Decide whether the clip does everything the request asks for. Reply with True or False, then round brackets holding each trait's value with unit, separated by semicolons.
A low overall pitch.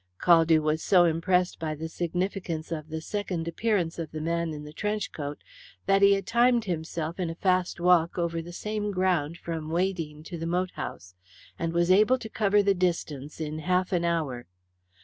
False (170 Hz)